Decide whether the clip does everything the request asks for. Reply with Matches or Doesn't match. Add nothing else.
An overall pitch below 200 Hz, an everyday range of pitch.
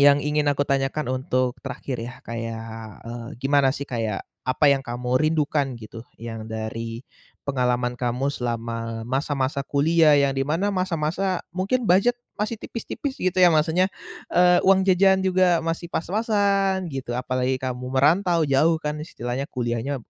Doesn't match